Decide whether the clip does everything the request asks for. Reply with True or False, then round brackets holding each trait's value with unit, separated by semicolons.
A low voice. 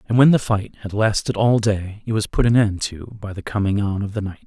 True (105 Hz)